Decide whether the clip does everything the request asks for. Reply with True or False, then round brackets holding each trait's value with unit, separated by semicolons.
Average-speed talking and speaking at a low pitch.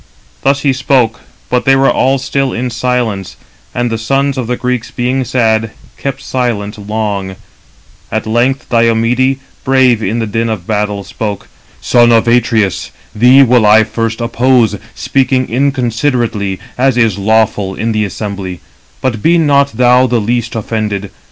True (150 wpm; 115 Hz)